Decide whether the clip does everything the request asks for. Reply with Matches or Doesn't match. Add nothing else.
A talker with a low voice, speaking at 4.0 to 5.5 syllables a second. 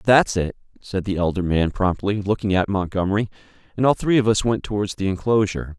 Doesn't match